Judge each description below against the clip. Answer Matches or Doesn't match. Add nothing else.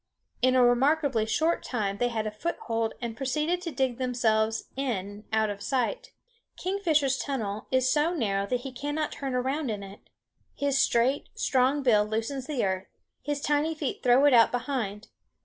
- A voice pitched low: Doesn't match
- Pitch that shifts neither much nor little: Matches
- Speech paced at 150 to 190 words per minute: Matches